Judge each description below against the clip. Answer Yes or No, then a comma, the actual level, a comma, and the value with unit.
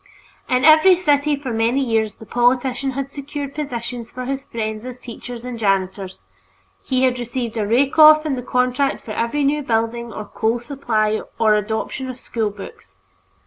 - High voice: Yes, high, 245 Hz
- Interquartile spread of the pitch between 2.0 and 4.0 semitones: Yes, average, 3.5 semitones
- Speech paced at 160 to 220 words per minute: Yes, average, 175 wpm